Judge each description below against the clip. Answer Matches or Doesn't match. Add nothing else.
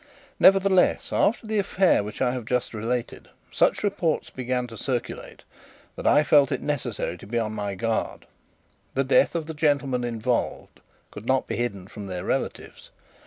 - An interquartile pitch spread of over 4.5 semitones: Matches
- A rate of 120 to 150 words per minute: Doesn't match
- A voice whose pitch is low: Matches